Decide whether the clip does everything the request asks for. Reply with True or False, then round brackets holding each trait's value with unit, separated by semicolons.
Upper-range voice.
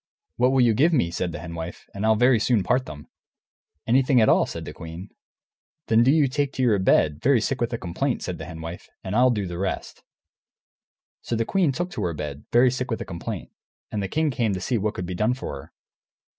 False (110 Hz)